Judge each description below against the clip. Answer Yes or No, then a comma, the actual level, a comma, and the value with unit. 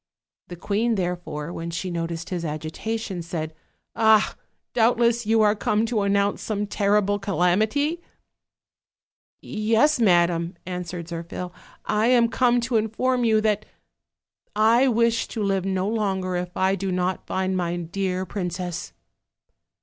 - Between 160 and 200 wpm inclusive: No, slow, 135 wpm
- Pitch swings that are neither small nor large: Yes, average, 3.8 semitones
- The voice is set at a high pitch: Yes, high, 195 Hz